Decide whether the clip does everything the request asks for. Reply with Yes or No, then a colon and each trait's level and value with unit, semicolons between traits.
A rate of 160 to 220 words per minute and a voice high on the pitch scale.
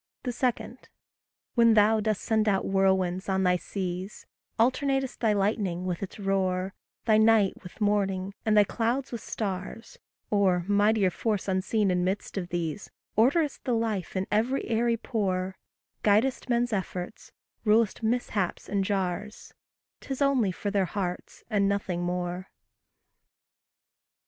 No: slow, 135 wpm; high, 205 Hz